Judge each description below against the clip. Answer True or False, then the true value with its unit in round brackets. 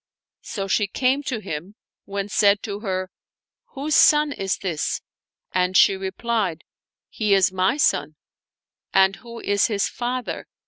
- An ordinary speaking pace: True (170 wpm)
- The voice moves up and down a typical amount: True (3.8 semitones)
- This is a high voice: True (200 Hz)